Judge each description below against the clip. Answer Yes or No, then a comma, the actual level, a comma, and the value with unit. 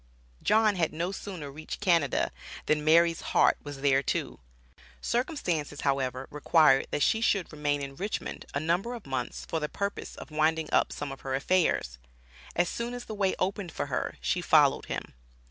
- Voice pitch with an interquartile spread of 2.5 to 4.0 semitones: No, average, 5.2 semitones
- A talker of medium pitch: Yes, medium, 160 Hz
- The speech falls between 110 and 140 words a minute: No, average, 180 wpm